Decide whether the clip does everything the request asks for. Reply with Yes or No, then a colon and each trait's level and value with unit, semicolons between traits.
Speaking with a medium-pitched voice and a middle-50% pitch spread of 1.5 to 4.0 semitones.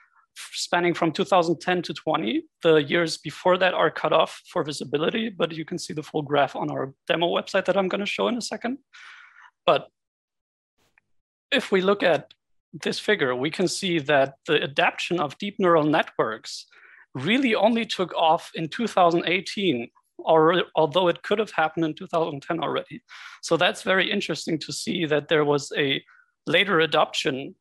No: medium, 175 Hz; average, 4.4 semitones